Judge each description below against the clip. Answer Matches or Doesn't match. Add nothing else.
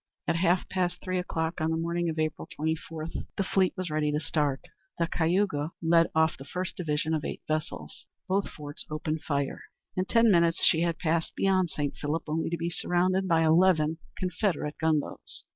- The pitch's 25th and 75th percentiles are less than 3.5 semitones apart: Matches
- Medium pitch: Matches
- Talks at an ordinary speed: Matches